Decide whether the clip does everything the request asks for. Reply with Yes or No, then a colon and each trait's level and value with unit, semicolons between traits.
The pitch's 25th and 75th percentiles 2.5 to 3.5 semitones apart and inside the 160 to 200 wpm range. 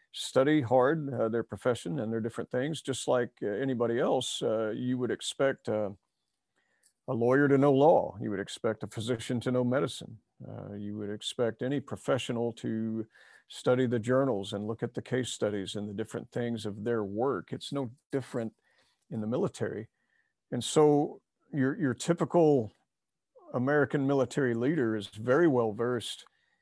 Yes: average, 3.2 semitones; average, 165 wpm